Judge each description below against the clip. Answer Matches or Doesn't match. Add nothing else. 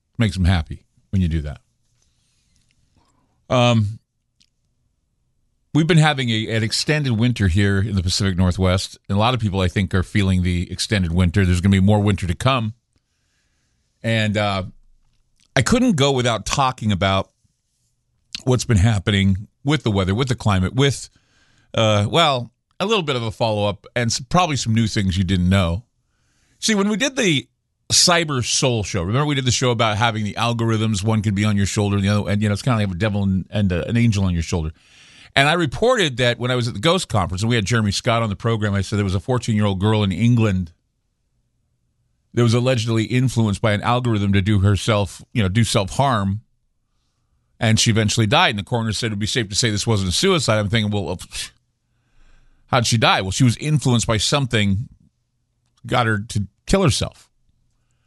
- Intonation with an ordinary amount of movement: Matches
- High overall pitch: Doesn't match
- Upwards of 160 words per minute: Matches